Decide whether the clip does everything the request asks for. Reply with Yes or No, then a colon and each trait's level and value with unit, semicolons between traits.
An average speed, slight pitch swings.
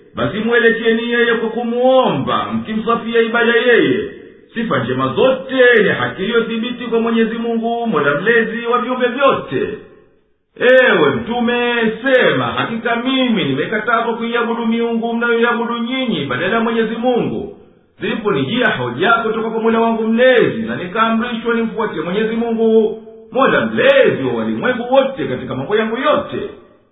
Yes: average, 125 wpm; narrow, 1.4 semitones